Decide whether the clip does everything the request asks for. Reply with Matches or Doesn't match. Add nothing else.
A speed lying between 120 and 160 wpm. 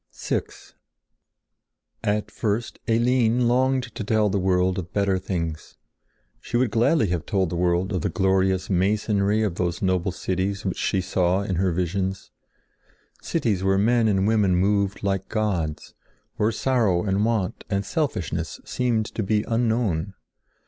Matches